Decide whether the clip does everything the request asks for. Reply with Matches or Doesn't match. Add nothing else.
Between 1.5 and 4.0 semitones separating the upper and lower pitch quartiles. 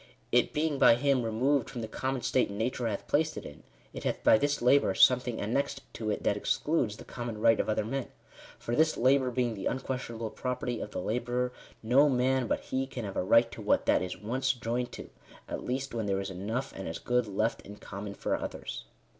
Matches